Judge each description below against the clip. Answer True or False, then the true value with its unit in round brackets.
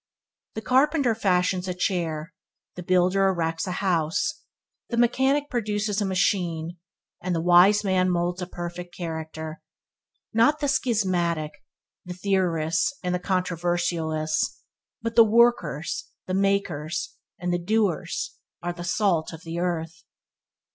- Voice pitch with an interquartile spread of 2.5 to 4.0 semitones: True (3.3 semitones)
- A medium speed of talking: False (130 wpm)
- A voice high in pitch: False (180 Hz)